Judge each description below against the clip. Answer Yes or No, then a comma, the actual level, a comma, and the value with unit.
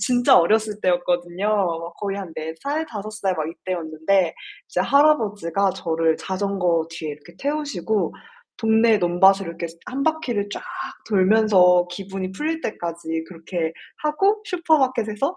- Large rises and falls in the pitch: No, average, 4.5 semitones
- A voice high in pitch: Yes, high, 195 Hz